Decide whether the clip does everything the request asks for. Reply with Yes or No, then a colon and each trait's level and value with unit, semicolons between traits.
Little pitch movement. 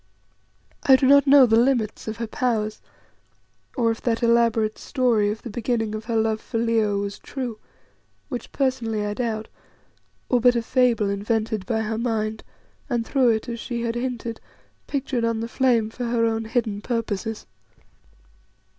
Yes: narrow, 1.9 semitones